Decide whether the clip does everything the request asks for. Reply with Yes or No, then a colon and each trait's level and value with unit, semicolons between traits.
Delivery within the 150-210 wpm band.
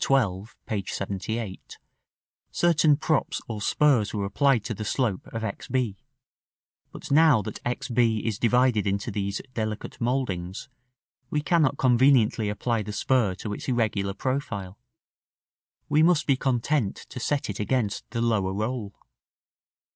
No: average, 140 wpm